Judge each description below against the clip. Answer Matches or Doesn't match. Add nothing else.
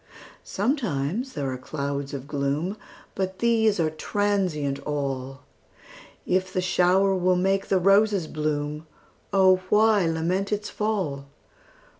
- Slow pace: Matches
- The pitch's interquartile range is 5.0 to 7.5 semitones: Matches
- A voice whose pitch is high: Doesn't match